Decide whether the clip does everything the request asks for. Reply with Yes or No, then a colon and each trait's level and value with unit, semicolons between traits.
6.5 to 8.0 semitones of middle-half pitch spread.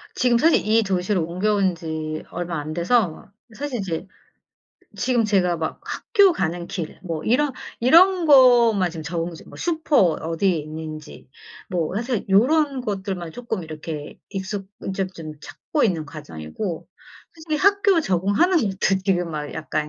Yes: wide, 6.9 semitones